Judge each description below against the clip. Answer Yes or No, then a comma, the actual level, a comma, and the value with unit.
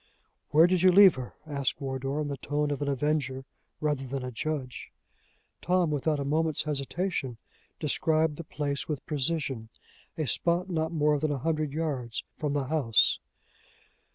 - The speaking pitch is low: No, medium, 150 Hz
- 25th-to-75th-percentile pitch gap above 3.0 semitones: No, average, 2.7 semitones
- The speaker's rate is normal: Yes, average, 160 wpm